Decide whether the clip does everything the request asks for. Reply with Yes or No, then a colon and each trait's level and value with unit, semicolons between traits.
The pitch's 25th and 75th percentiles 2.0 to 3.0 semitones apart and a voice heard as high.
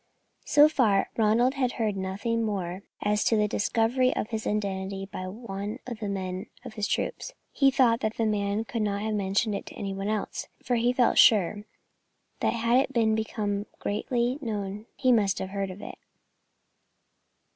Yes: average, 2.7 semitones; high, 215 Hz